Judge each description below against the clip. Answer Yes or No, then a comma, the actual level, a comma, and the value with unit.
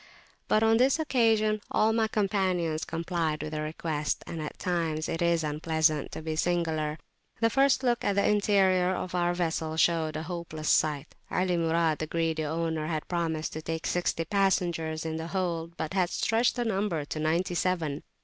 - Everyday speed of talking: Yes, average, 180 wpm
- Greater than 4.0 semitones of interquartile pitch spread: No, average, 3.2 semitones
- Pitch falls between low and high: Yes, medium, 170 Hz